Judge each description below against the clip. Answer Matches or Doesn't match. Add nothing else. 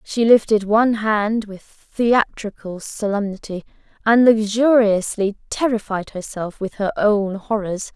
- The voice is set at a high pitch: Matches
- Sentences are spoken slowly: Matches